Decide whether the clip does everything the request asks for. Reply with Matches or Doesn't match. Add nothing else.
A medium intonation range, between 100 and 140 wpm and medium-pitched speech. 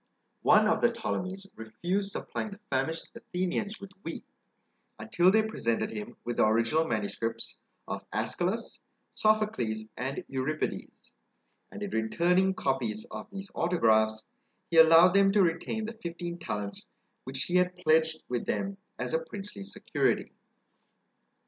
Doesn't match